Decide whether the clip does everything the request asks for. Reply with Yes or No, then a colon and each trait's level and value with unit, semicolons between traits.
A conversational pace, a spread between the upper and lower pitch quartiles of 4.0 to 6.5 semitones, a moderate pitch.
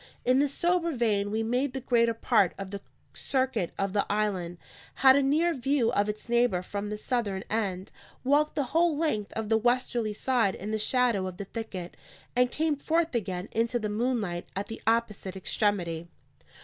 No: average, 185 wpm; average, 4.4 semitones; high, 225 Hz